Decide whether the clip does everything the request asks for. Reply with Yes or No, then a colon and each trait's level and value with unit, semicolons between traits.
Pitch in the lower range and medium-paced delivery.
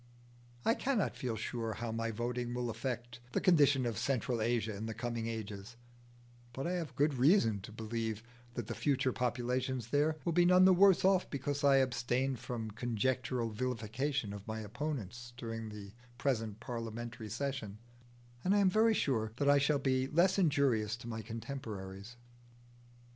Yes: low, 120 Hz; average, 165 wpm